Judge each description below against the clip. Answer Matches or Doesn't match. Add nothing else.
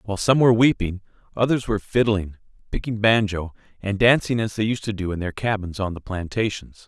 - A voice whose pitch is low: Matches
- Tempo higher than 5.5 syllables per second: Matches